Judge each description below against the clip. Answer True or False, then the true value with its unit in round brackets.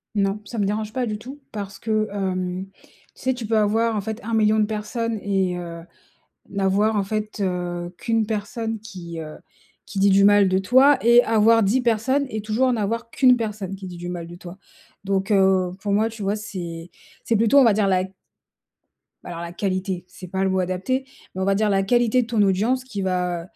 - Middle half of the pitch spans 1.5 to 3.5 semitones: True (3.1 semitones)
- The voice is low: False (205 Hz)